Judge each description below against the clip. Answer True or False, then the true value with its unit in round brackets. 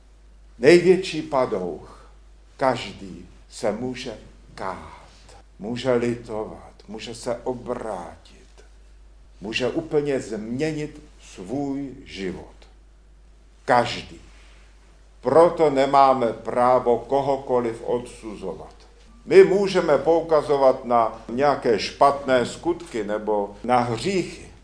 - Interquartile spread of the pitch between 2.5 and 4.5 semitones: False (5.6 semitones)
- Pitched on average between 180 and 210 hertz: False (120 Hz)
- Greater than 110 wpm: False (80 wpm)